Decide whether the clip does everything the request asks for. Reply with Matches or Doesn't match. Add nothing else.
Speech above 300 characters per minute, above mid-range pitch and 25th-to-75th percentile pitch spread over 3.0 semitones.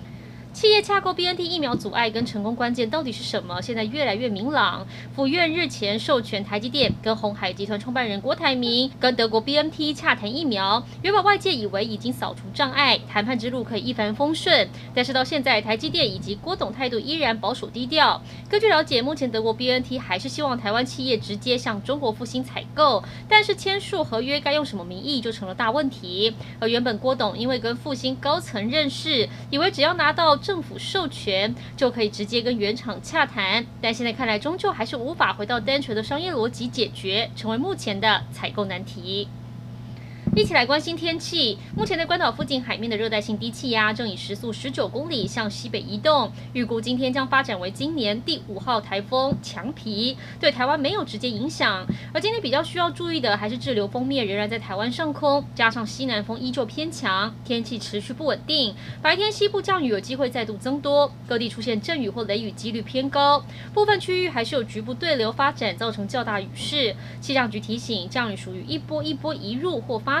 Matches